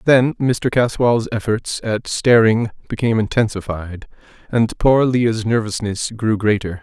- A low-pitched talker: Yes, low, 115 Hz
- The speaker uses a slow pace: Yes, slow, 125 wpm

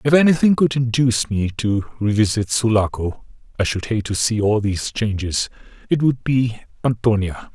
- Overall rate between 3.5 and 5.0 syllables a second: Yes, 4.0 syllables/s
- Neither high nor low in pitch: No, low, 115 Hz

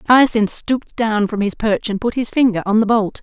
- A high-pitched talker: Yes, high, 220 Hz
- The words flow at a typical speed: No, fast, 240 wpm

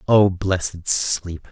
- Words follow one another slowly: Yes, slow, 120 wpm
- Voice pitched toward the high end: No, very low, 90 Hz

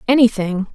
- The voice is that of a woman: Yes, female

